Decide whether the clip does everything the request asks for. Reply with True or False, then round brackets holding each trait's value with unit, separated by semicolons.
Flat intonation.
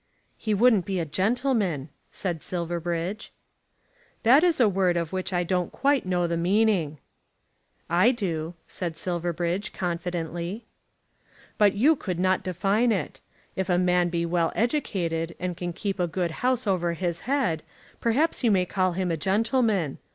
False (3.8 semitones)